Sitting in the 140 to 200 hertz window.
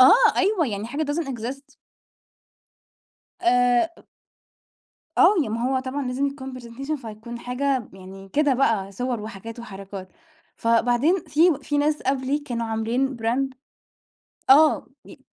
No: very high, 255 Hz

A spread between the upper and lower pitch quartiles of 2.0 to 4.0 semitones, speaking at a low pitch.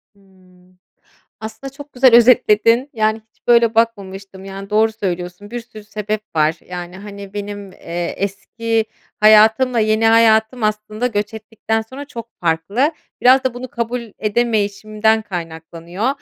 No: average, 2.8 semitones; high, 215 Hz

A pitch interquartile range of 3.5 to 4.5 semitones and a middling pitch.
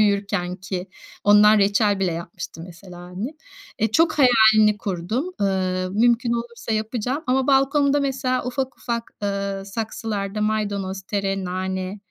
No: average, 3.8 semitones; high, 205 Hz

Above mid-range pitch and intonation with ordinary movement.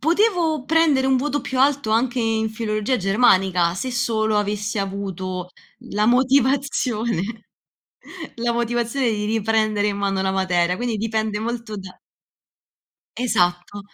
Yes: high, 220 Hz; average, 3.9 semitones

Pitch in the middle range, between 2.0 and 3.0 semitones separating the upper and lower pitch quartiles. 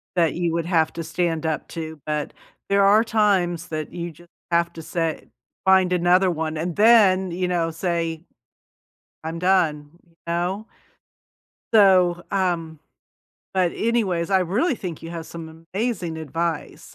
Yes: medium, 175 Hz; narrow, 2.5 semitones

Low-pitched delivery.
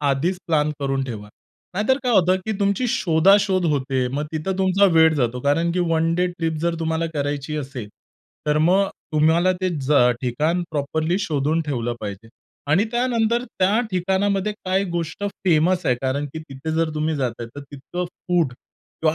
No: medium, 160 Hz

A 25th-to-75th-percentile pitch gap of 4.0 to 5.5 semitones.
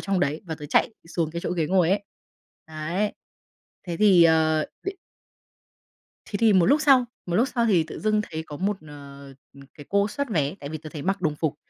Yes: average, 4.7 semitones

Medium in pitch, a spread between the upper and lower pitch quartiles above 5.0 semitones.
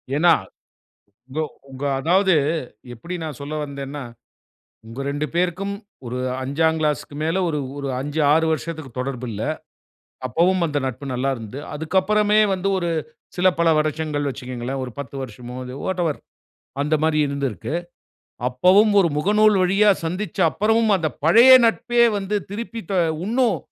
Yes: medium, 160 Hz; wide, 5.5 semitones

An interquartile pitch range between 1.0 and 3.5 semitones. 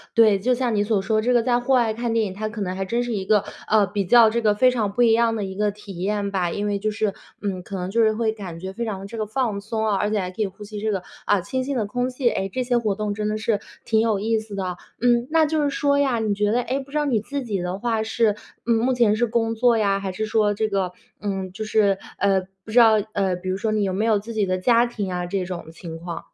Yes: average, 2.9 semitones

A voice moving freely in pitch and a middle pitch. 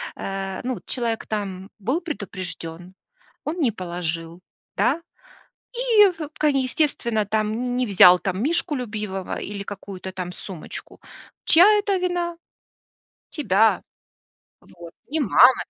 No: wide, 7.9 semitones; high, 215 Hz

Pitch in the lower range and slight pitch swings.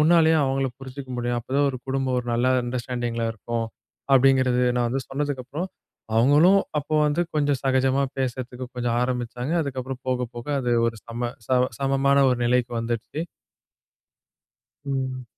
Yes: low, 130 Hz; narrow, 2.0 semitones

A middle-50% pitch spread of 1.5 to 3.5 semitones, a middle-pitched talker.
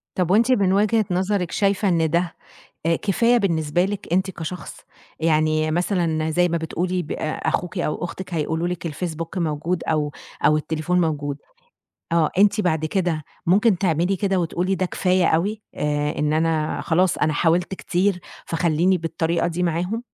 Yes: average, 2.8 semitones; medium, 175 Hz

